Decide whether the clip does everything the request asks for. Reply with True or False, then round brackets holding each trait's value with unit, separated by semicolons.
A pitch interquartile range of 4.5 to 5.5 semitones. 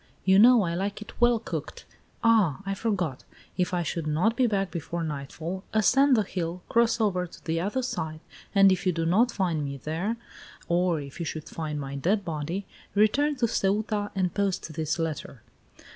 True (4.8 semitones)